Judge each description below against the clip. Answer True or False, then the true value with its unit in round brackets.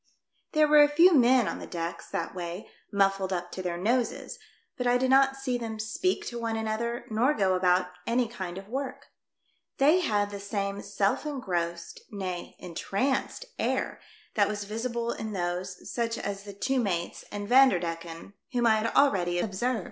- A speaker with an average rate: True (180 wpm)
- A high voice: True (215 Hz)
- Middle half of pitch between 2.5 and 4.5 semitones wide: False (5.0 semitones)